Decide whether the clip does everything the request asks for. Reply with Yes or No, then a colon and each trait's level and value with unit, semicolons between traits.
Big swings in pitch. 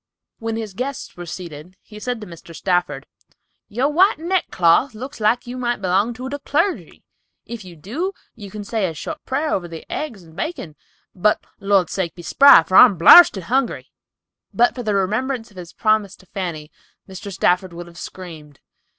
Yes: wide, 5.9 semitones